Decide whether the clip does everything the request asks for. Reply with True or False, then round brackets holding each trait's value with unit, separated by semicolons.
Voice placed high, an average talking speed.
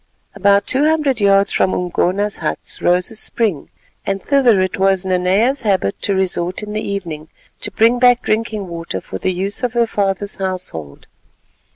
True (200 Hz; 170 wpm)